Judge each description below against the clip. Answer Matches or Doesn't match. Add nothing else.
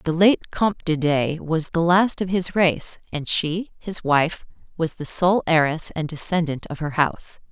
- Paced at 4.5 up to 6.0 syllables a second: Doesn't match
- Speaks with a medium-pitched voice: Matches